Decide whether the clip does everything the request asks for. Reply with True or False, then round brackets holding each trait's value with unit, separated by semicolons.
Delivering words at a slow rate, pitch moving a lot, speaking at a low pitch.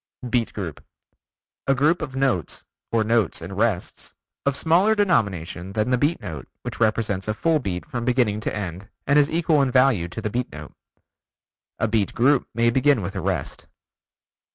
False (175 wpm; 5.7 semitones; 115 Hz)